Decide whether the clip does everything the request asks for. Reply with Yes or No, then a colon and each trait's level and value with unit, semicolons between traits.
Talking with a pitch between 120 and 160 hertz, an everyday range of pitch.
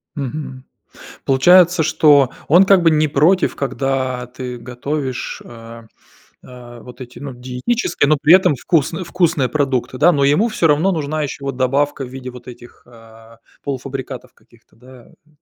Yes: low, 135 Hz; average, 3.7 semitones